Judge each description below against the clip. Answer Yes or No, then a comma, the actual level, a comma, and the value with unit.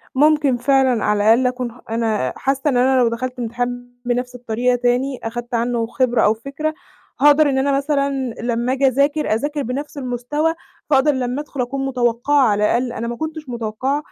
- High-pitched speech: Yes, very high, 250 Hz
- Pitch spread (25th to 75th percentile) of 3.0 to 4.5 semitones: No, narrow, 2.6 semitones